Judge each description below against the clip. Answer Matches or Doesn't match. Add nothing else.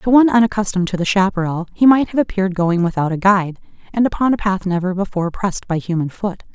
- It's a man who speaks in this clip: Doesn't match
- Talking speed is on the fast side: Matches